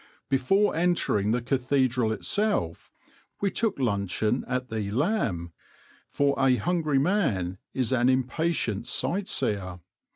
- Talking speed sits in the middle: No, slow, 120 wpm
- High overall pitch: No, low, 130 Hz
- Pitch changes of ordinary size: No, wide, 7.3 semitones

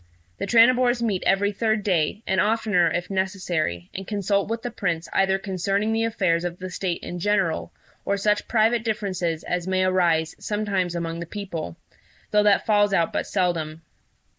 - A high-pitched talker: Yes, high, 195 Hz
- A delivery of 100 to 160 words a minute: No, average, 170 wpm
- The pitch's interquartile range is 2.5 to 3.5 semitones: Yes, average, 3.2 semitones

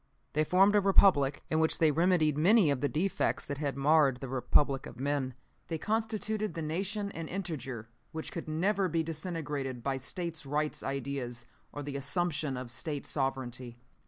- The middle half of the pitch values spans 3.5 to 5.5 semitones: Yes, average, 4.4 semitones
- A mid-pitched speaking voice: Yes, medium, 150 Hz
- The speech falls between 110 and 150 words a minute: No, average, 170 wpm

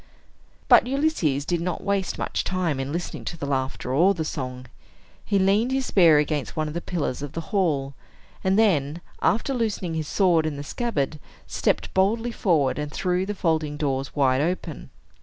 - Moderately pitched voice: Yes, medium, 165 Hz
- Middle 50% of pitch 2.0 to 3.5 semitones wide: No, average, 5.0 semitones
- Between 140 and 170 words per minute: No, average, 180 wpm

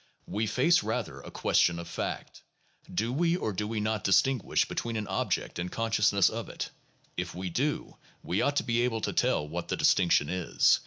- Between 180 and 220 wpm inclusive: Yes, average, 195 wpm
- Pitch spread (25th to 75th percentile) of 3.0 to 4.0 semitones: No, average, 4.5 semitones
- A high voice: No, low, 105 Hz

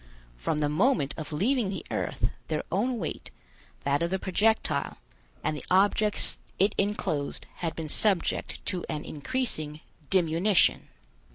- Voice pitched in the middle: Yes, medium, 180 Hz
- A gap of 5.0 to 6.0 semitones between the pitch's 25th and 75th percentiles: Yes, wide, 5.5 semitones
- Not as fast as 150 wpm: Yes, slow, 135 wpm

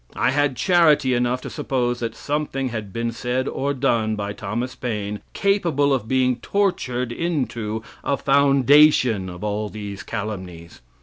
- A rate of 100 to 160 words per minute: Yes, average, 145 wpm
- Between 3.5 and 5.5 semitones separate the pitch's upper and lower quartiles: Yes, average, 4.5 semitones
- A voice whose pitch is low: Yes, low, 125 Hz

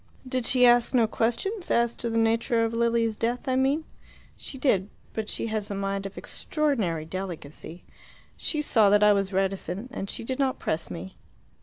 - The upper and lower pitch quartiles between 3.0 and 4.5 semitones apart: Yes, average, 4.2 semitones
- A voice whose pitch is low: No, high, 225 Hz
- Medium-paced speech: Yes, average, 185 wpm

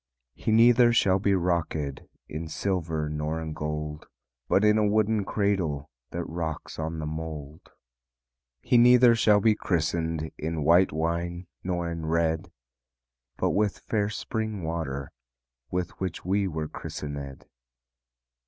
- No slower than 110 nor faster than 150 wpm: Yes, slow, 135 wpm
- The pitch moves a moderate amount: Yes, average, 4.5 semitones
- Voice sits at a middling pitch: No, very low, 85 Hz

